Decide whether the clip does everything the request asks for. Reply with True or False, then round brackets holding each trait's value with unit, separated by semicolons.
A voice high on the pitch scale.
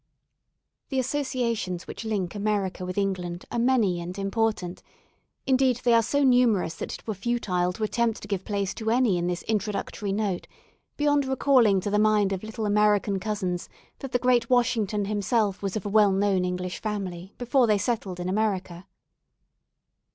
True (210 Hz)